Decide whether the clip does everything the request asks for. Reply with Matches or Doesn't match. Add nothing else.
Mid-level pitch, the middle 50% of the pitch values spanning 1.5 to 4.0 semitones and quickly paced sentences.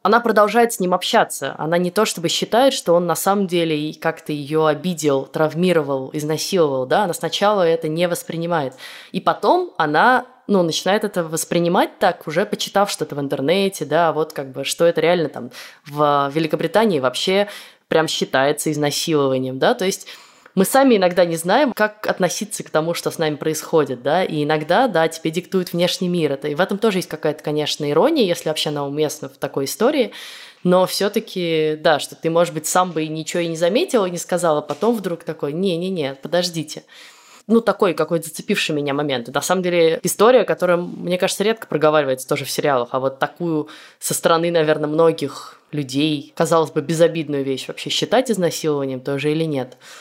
Matches